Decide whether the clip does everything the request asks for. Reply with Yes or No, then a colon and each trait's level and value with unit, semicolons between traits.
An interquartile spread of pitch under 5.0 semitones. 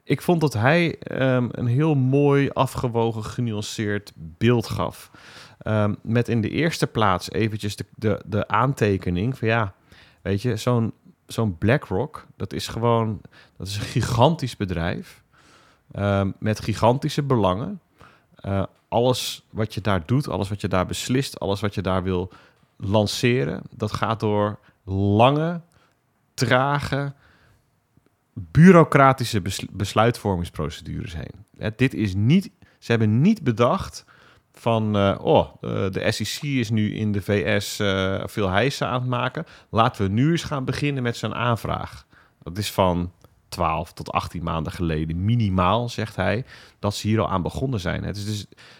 Yes: average, 4.3 semitones